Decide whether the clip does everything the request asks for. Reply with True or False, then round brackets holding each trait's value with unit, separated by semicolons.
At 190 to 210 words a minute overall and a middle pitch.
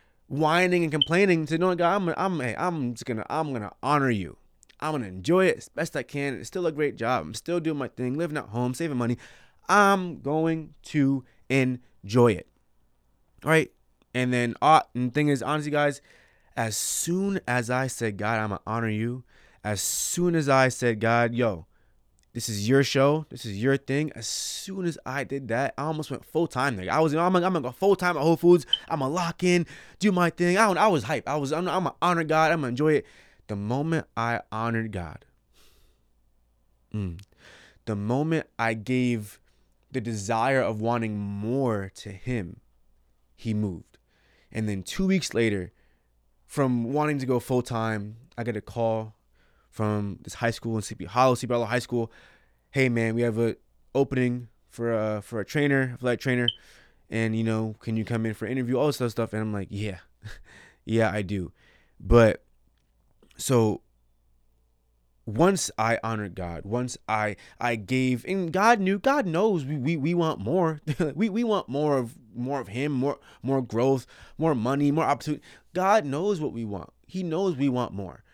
False (195 wpm; 125 Hz)